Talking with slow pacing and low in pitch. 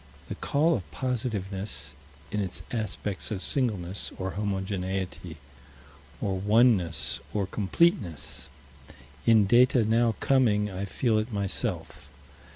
Yes: slow, 110 wpm; low, 105 Hz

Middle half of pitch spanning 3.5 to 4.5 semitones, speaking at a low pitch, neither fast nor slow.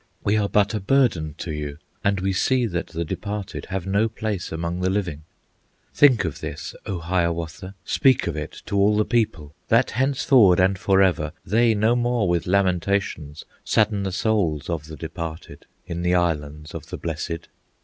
Yes: average, 4.1 semitones; very low, 95 Hz; average, 175 wpm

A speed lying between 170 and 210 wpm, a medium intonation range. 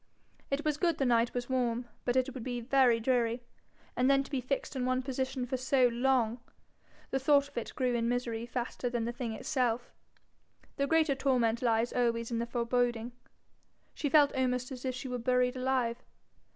No: average, 190 wpm; narrow, 1.9 semitones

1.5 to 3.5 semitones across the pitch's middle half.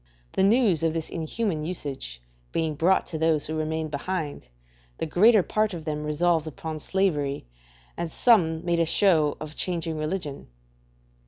Yes: average, 3.0 semitones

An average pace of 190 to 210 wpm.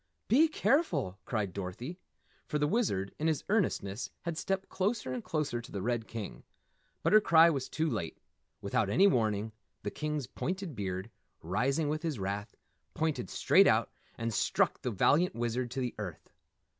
No: average, 170 wpm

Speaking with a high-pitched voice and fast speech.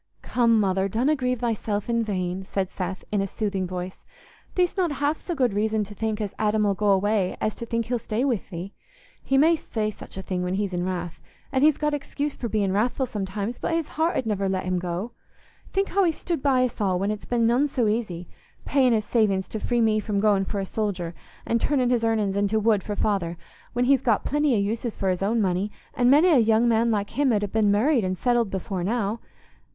Yes: high, 215 Hz; fast, 225 wpm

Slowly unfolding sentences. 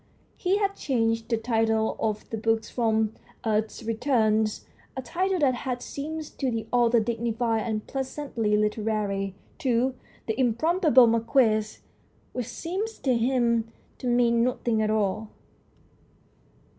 Yes: slow, 130 wpm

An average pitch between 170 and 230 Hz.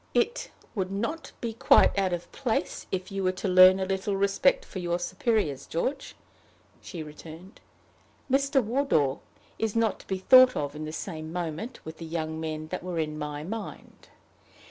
Yes: medium, 185 Hz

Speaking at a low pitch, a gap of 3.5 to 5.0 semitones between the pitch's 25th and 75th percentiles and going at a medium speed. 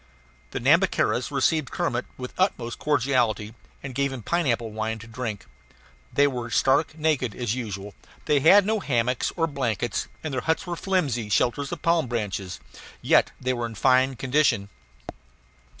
Yes: low, 125 Hz; average, 4.5 semitones; average, 160 wpm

